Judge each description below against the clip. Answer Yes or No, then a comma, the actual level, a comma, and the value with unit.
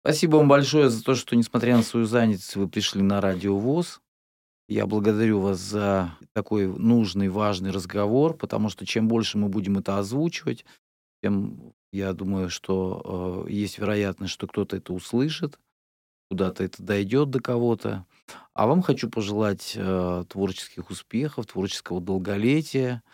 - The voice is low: Yes, low, 105 Hz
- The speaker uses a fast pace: No, average, 145 wpm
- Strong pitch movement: No, average, 3.8 semitones